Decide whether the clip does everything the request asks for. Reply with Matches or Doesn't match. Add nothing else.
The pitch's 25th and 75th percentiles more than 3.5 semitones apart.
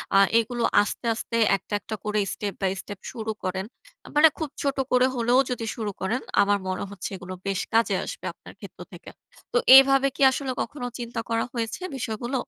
Matches